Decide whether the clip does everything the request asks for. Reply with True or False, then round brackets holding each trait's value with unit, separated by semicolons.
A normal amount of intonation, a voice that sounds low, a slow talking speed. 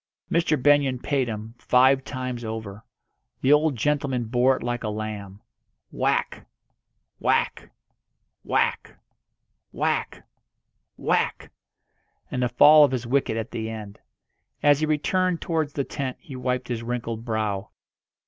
True (4.2 semitones; 125 Hz; 130 wpm)